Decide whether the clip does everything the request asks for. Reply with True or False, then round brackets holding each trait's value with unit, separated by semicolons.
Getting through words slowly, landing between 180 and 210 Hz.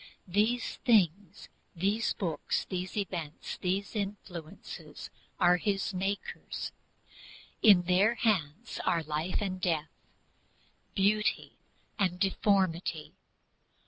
True (90 wpm; 190 Hz)